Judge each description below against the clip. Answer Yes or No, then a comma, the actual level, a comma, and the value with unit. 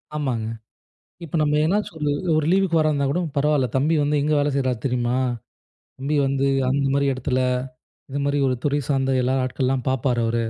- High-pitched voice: No, medium, 140 Hz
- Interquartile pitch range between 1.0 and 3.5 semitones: Yes, narrow, 2.5 semitones